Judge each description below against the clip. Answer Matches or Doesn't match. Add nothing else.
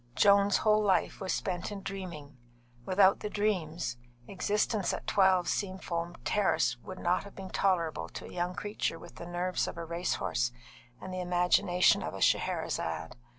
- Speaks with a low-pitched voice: Doesn't match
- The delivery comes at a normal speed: Matches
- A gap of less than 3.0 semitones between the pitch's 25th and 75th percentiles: Matches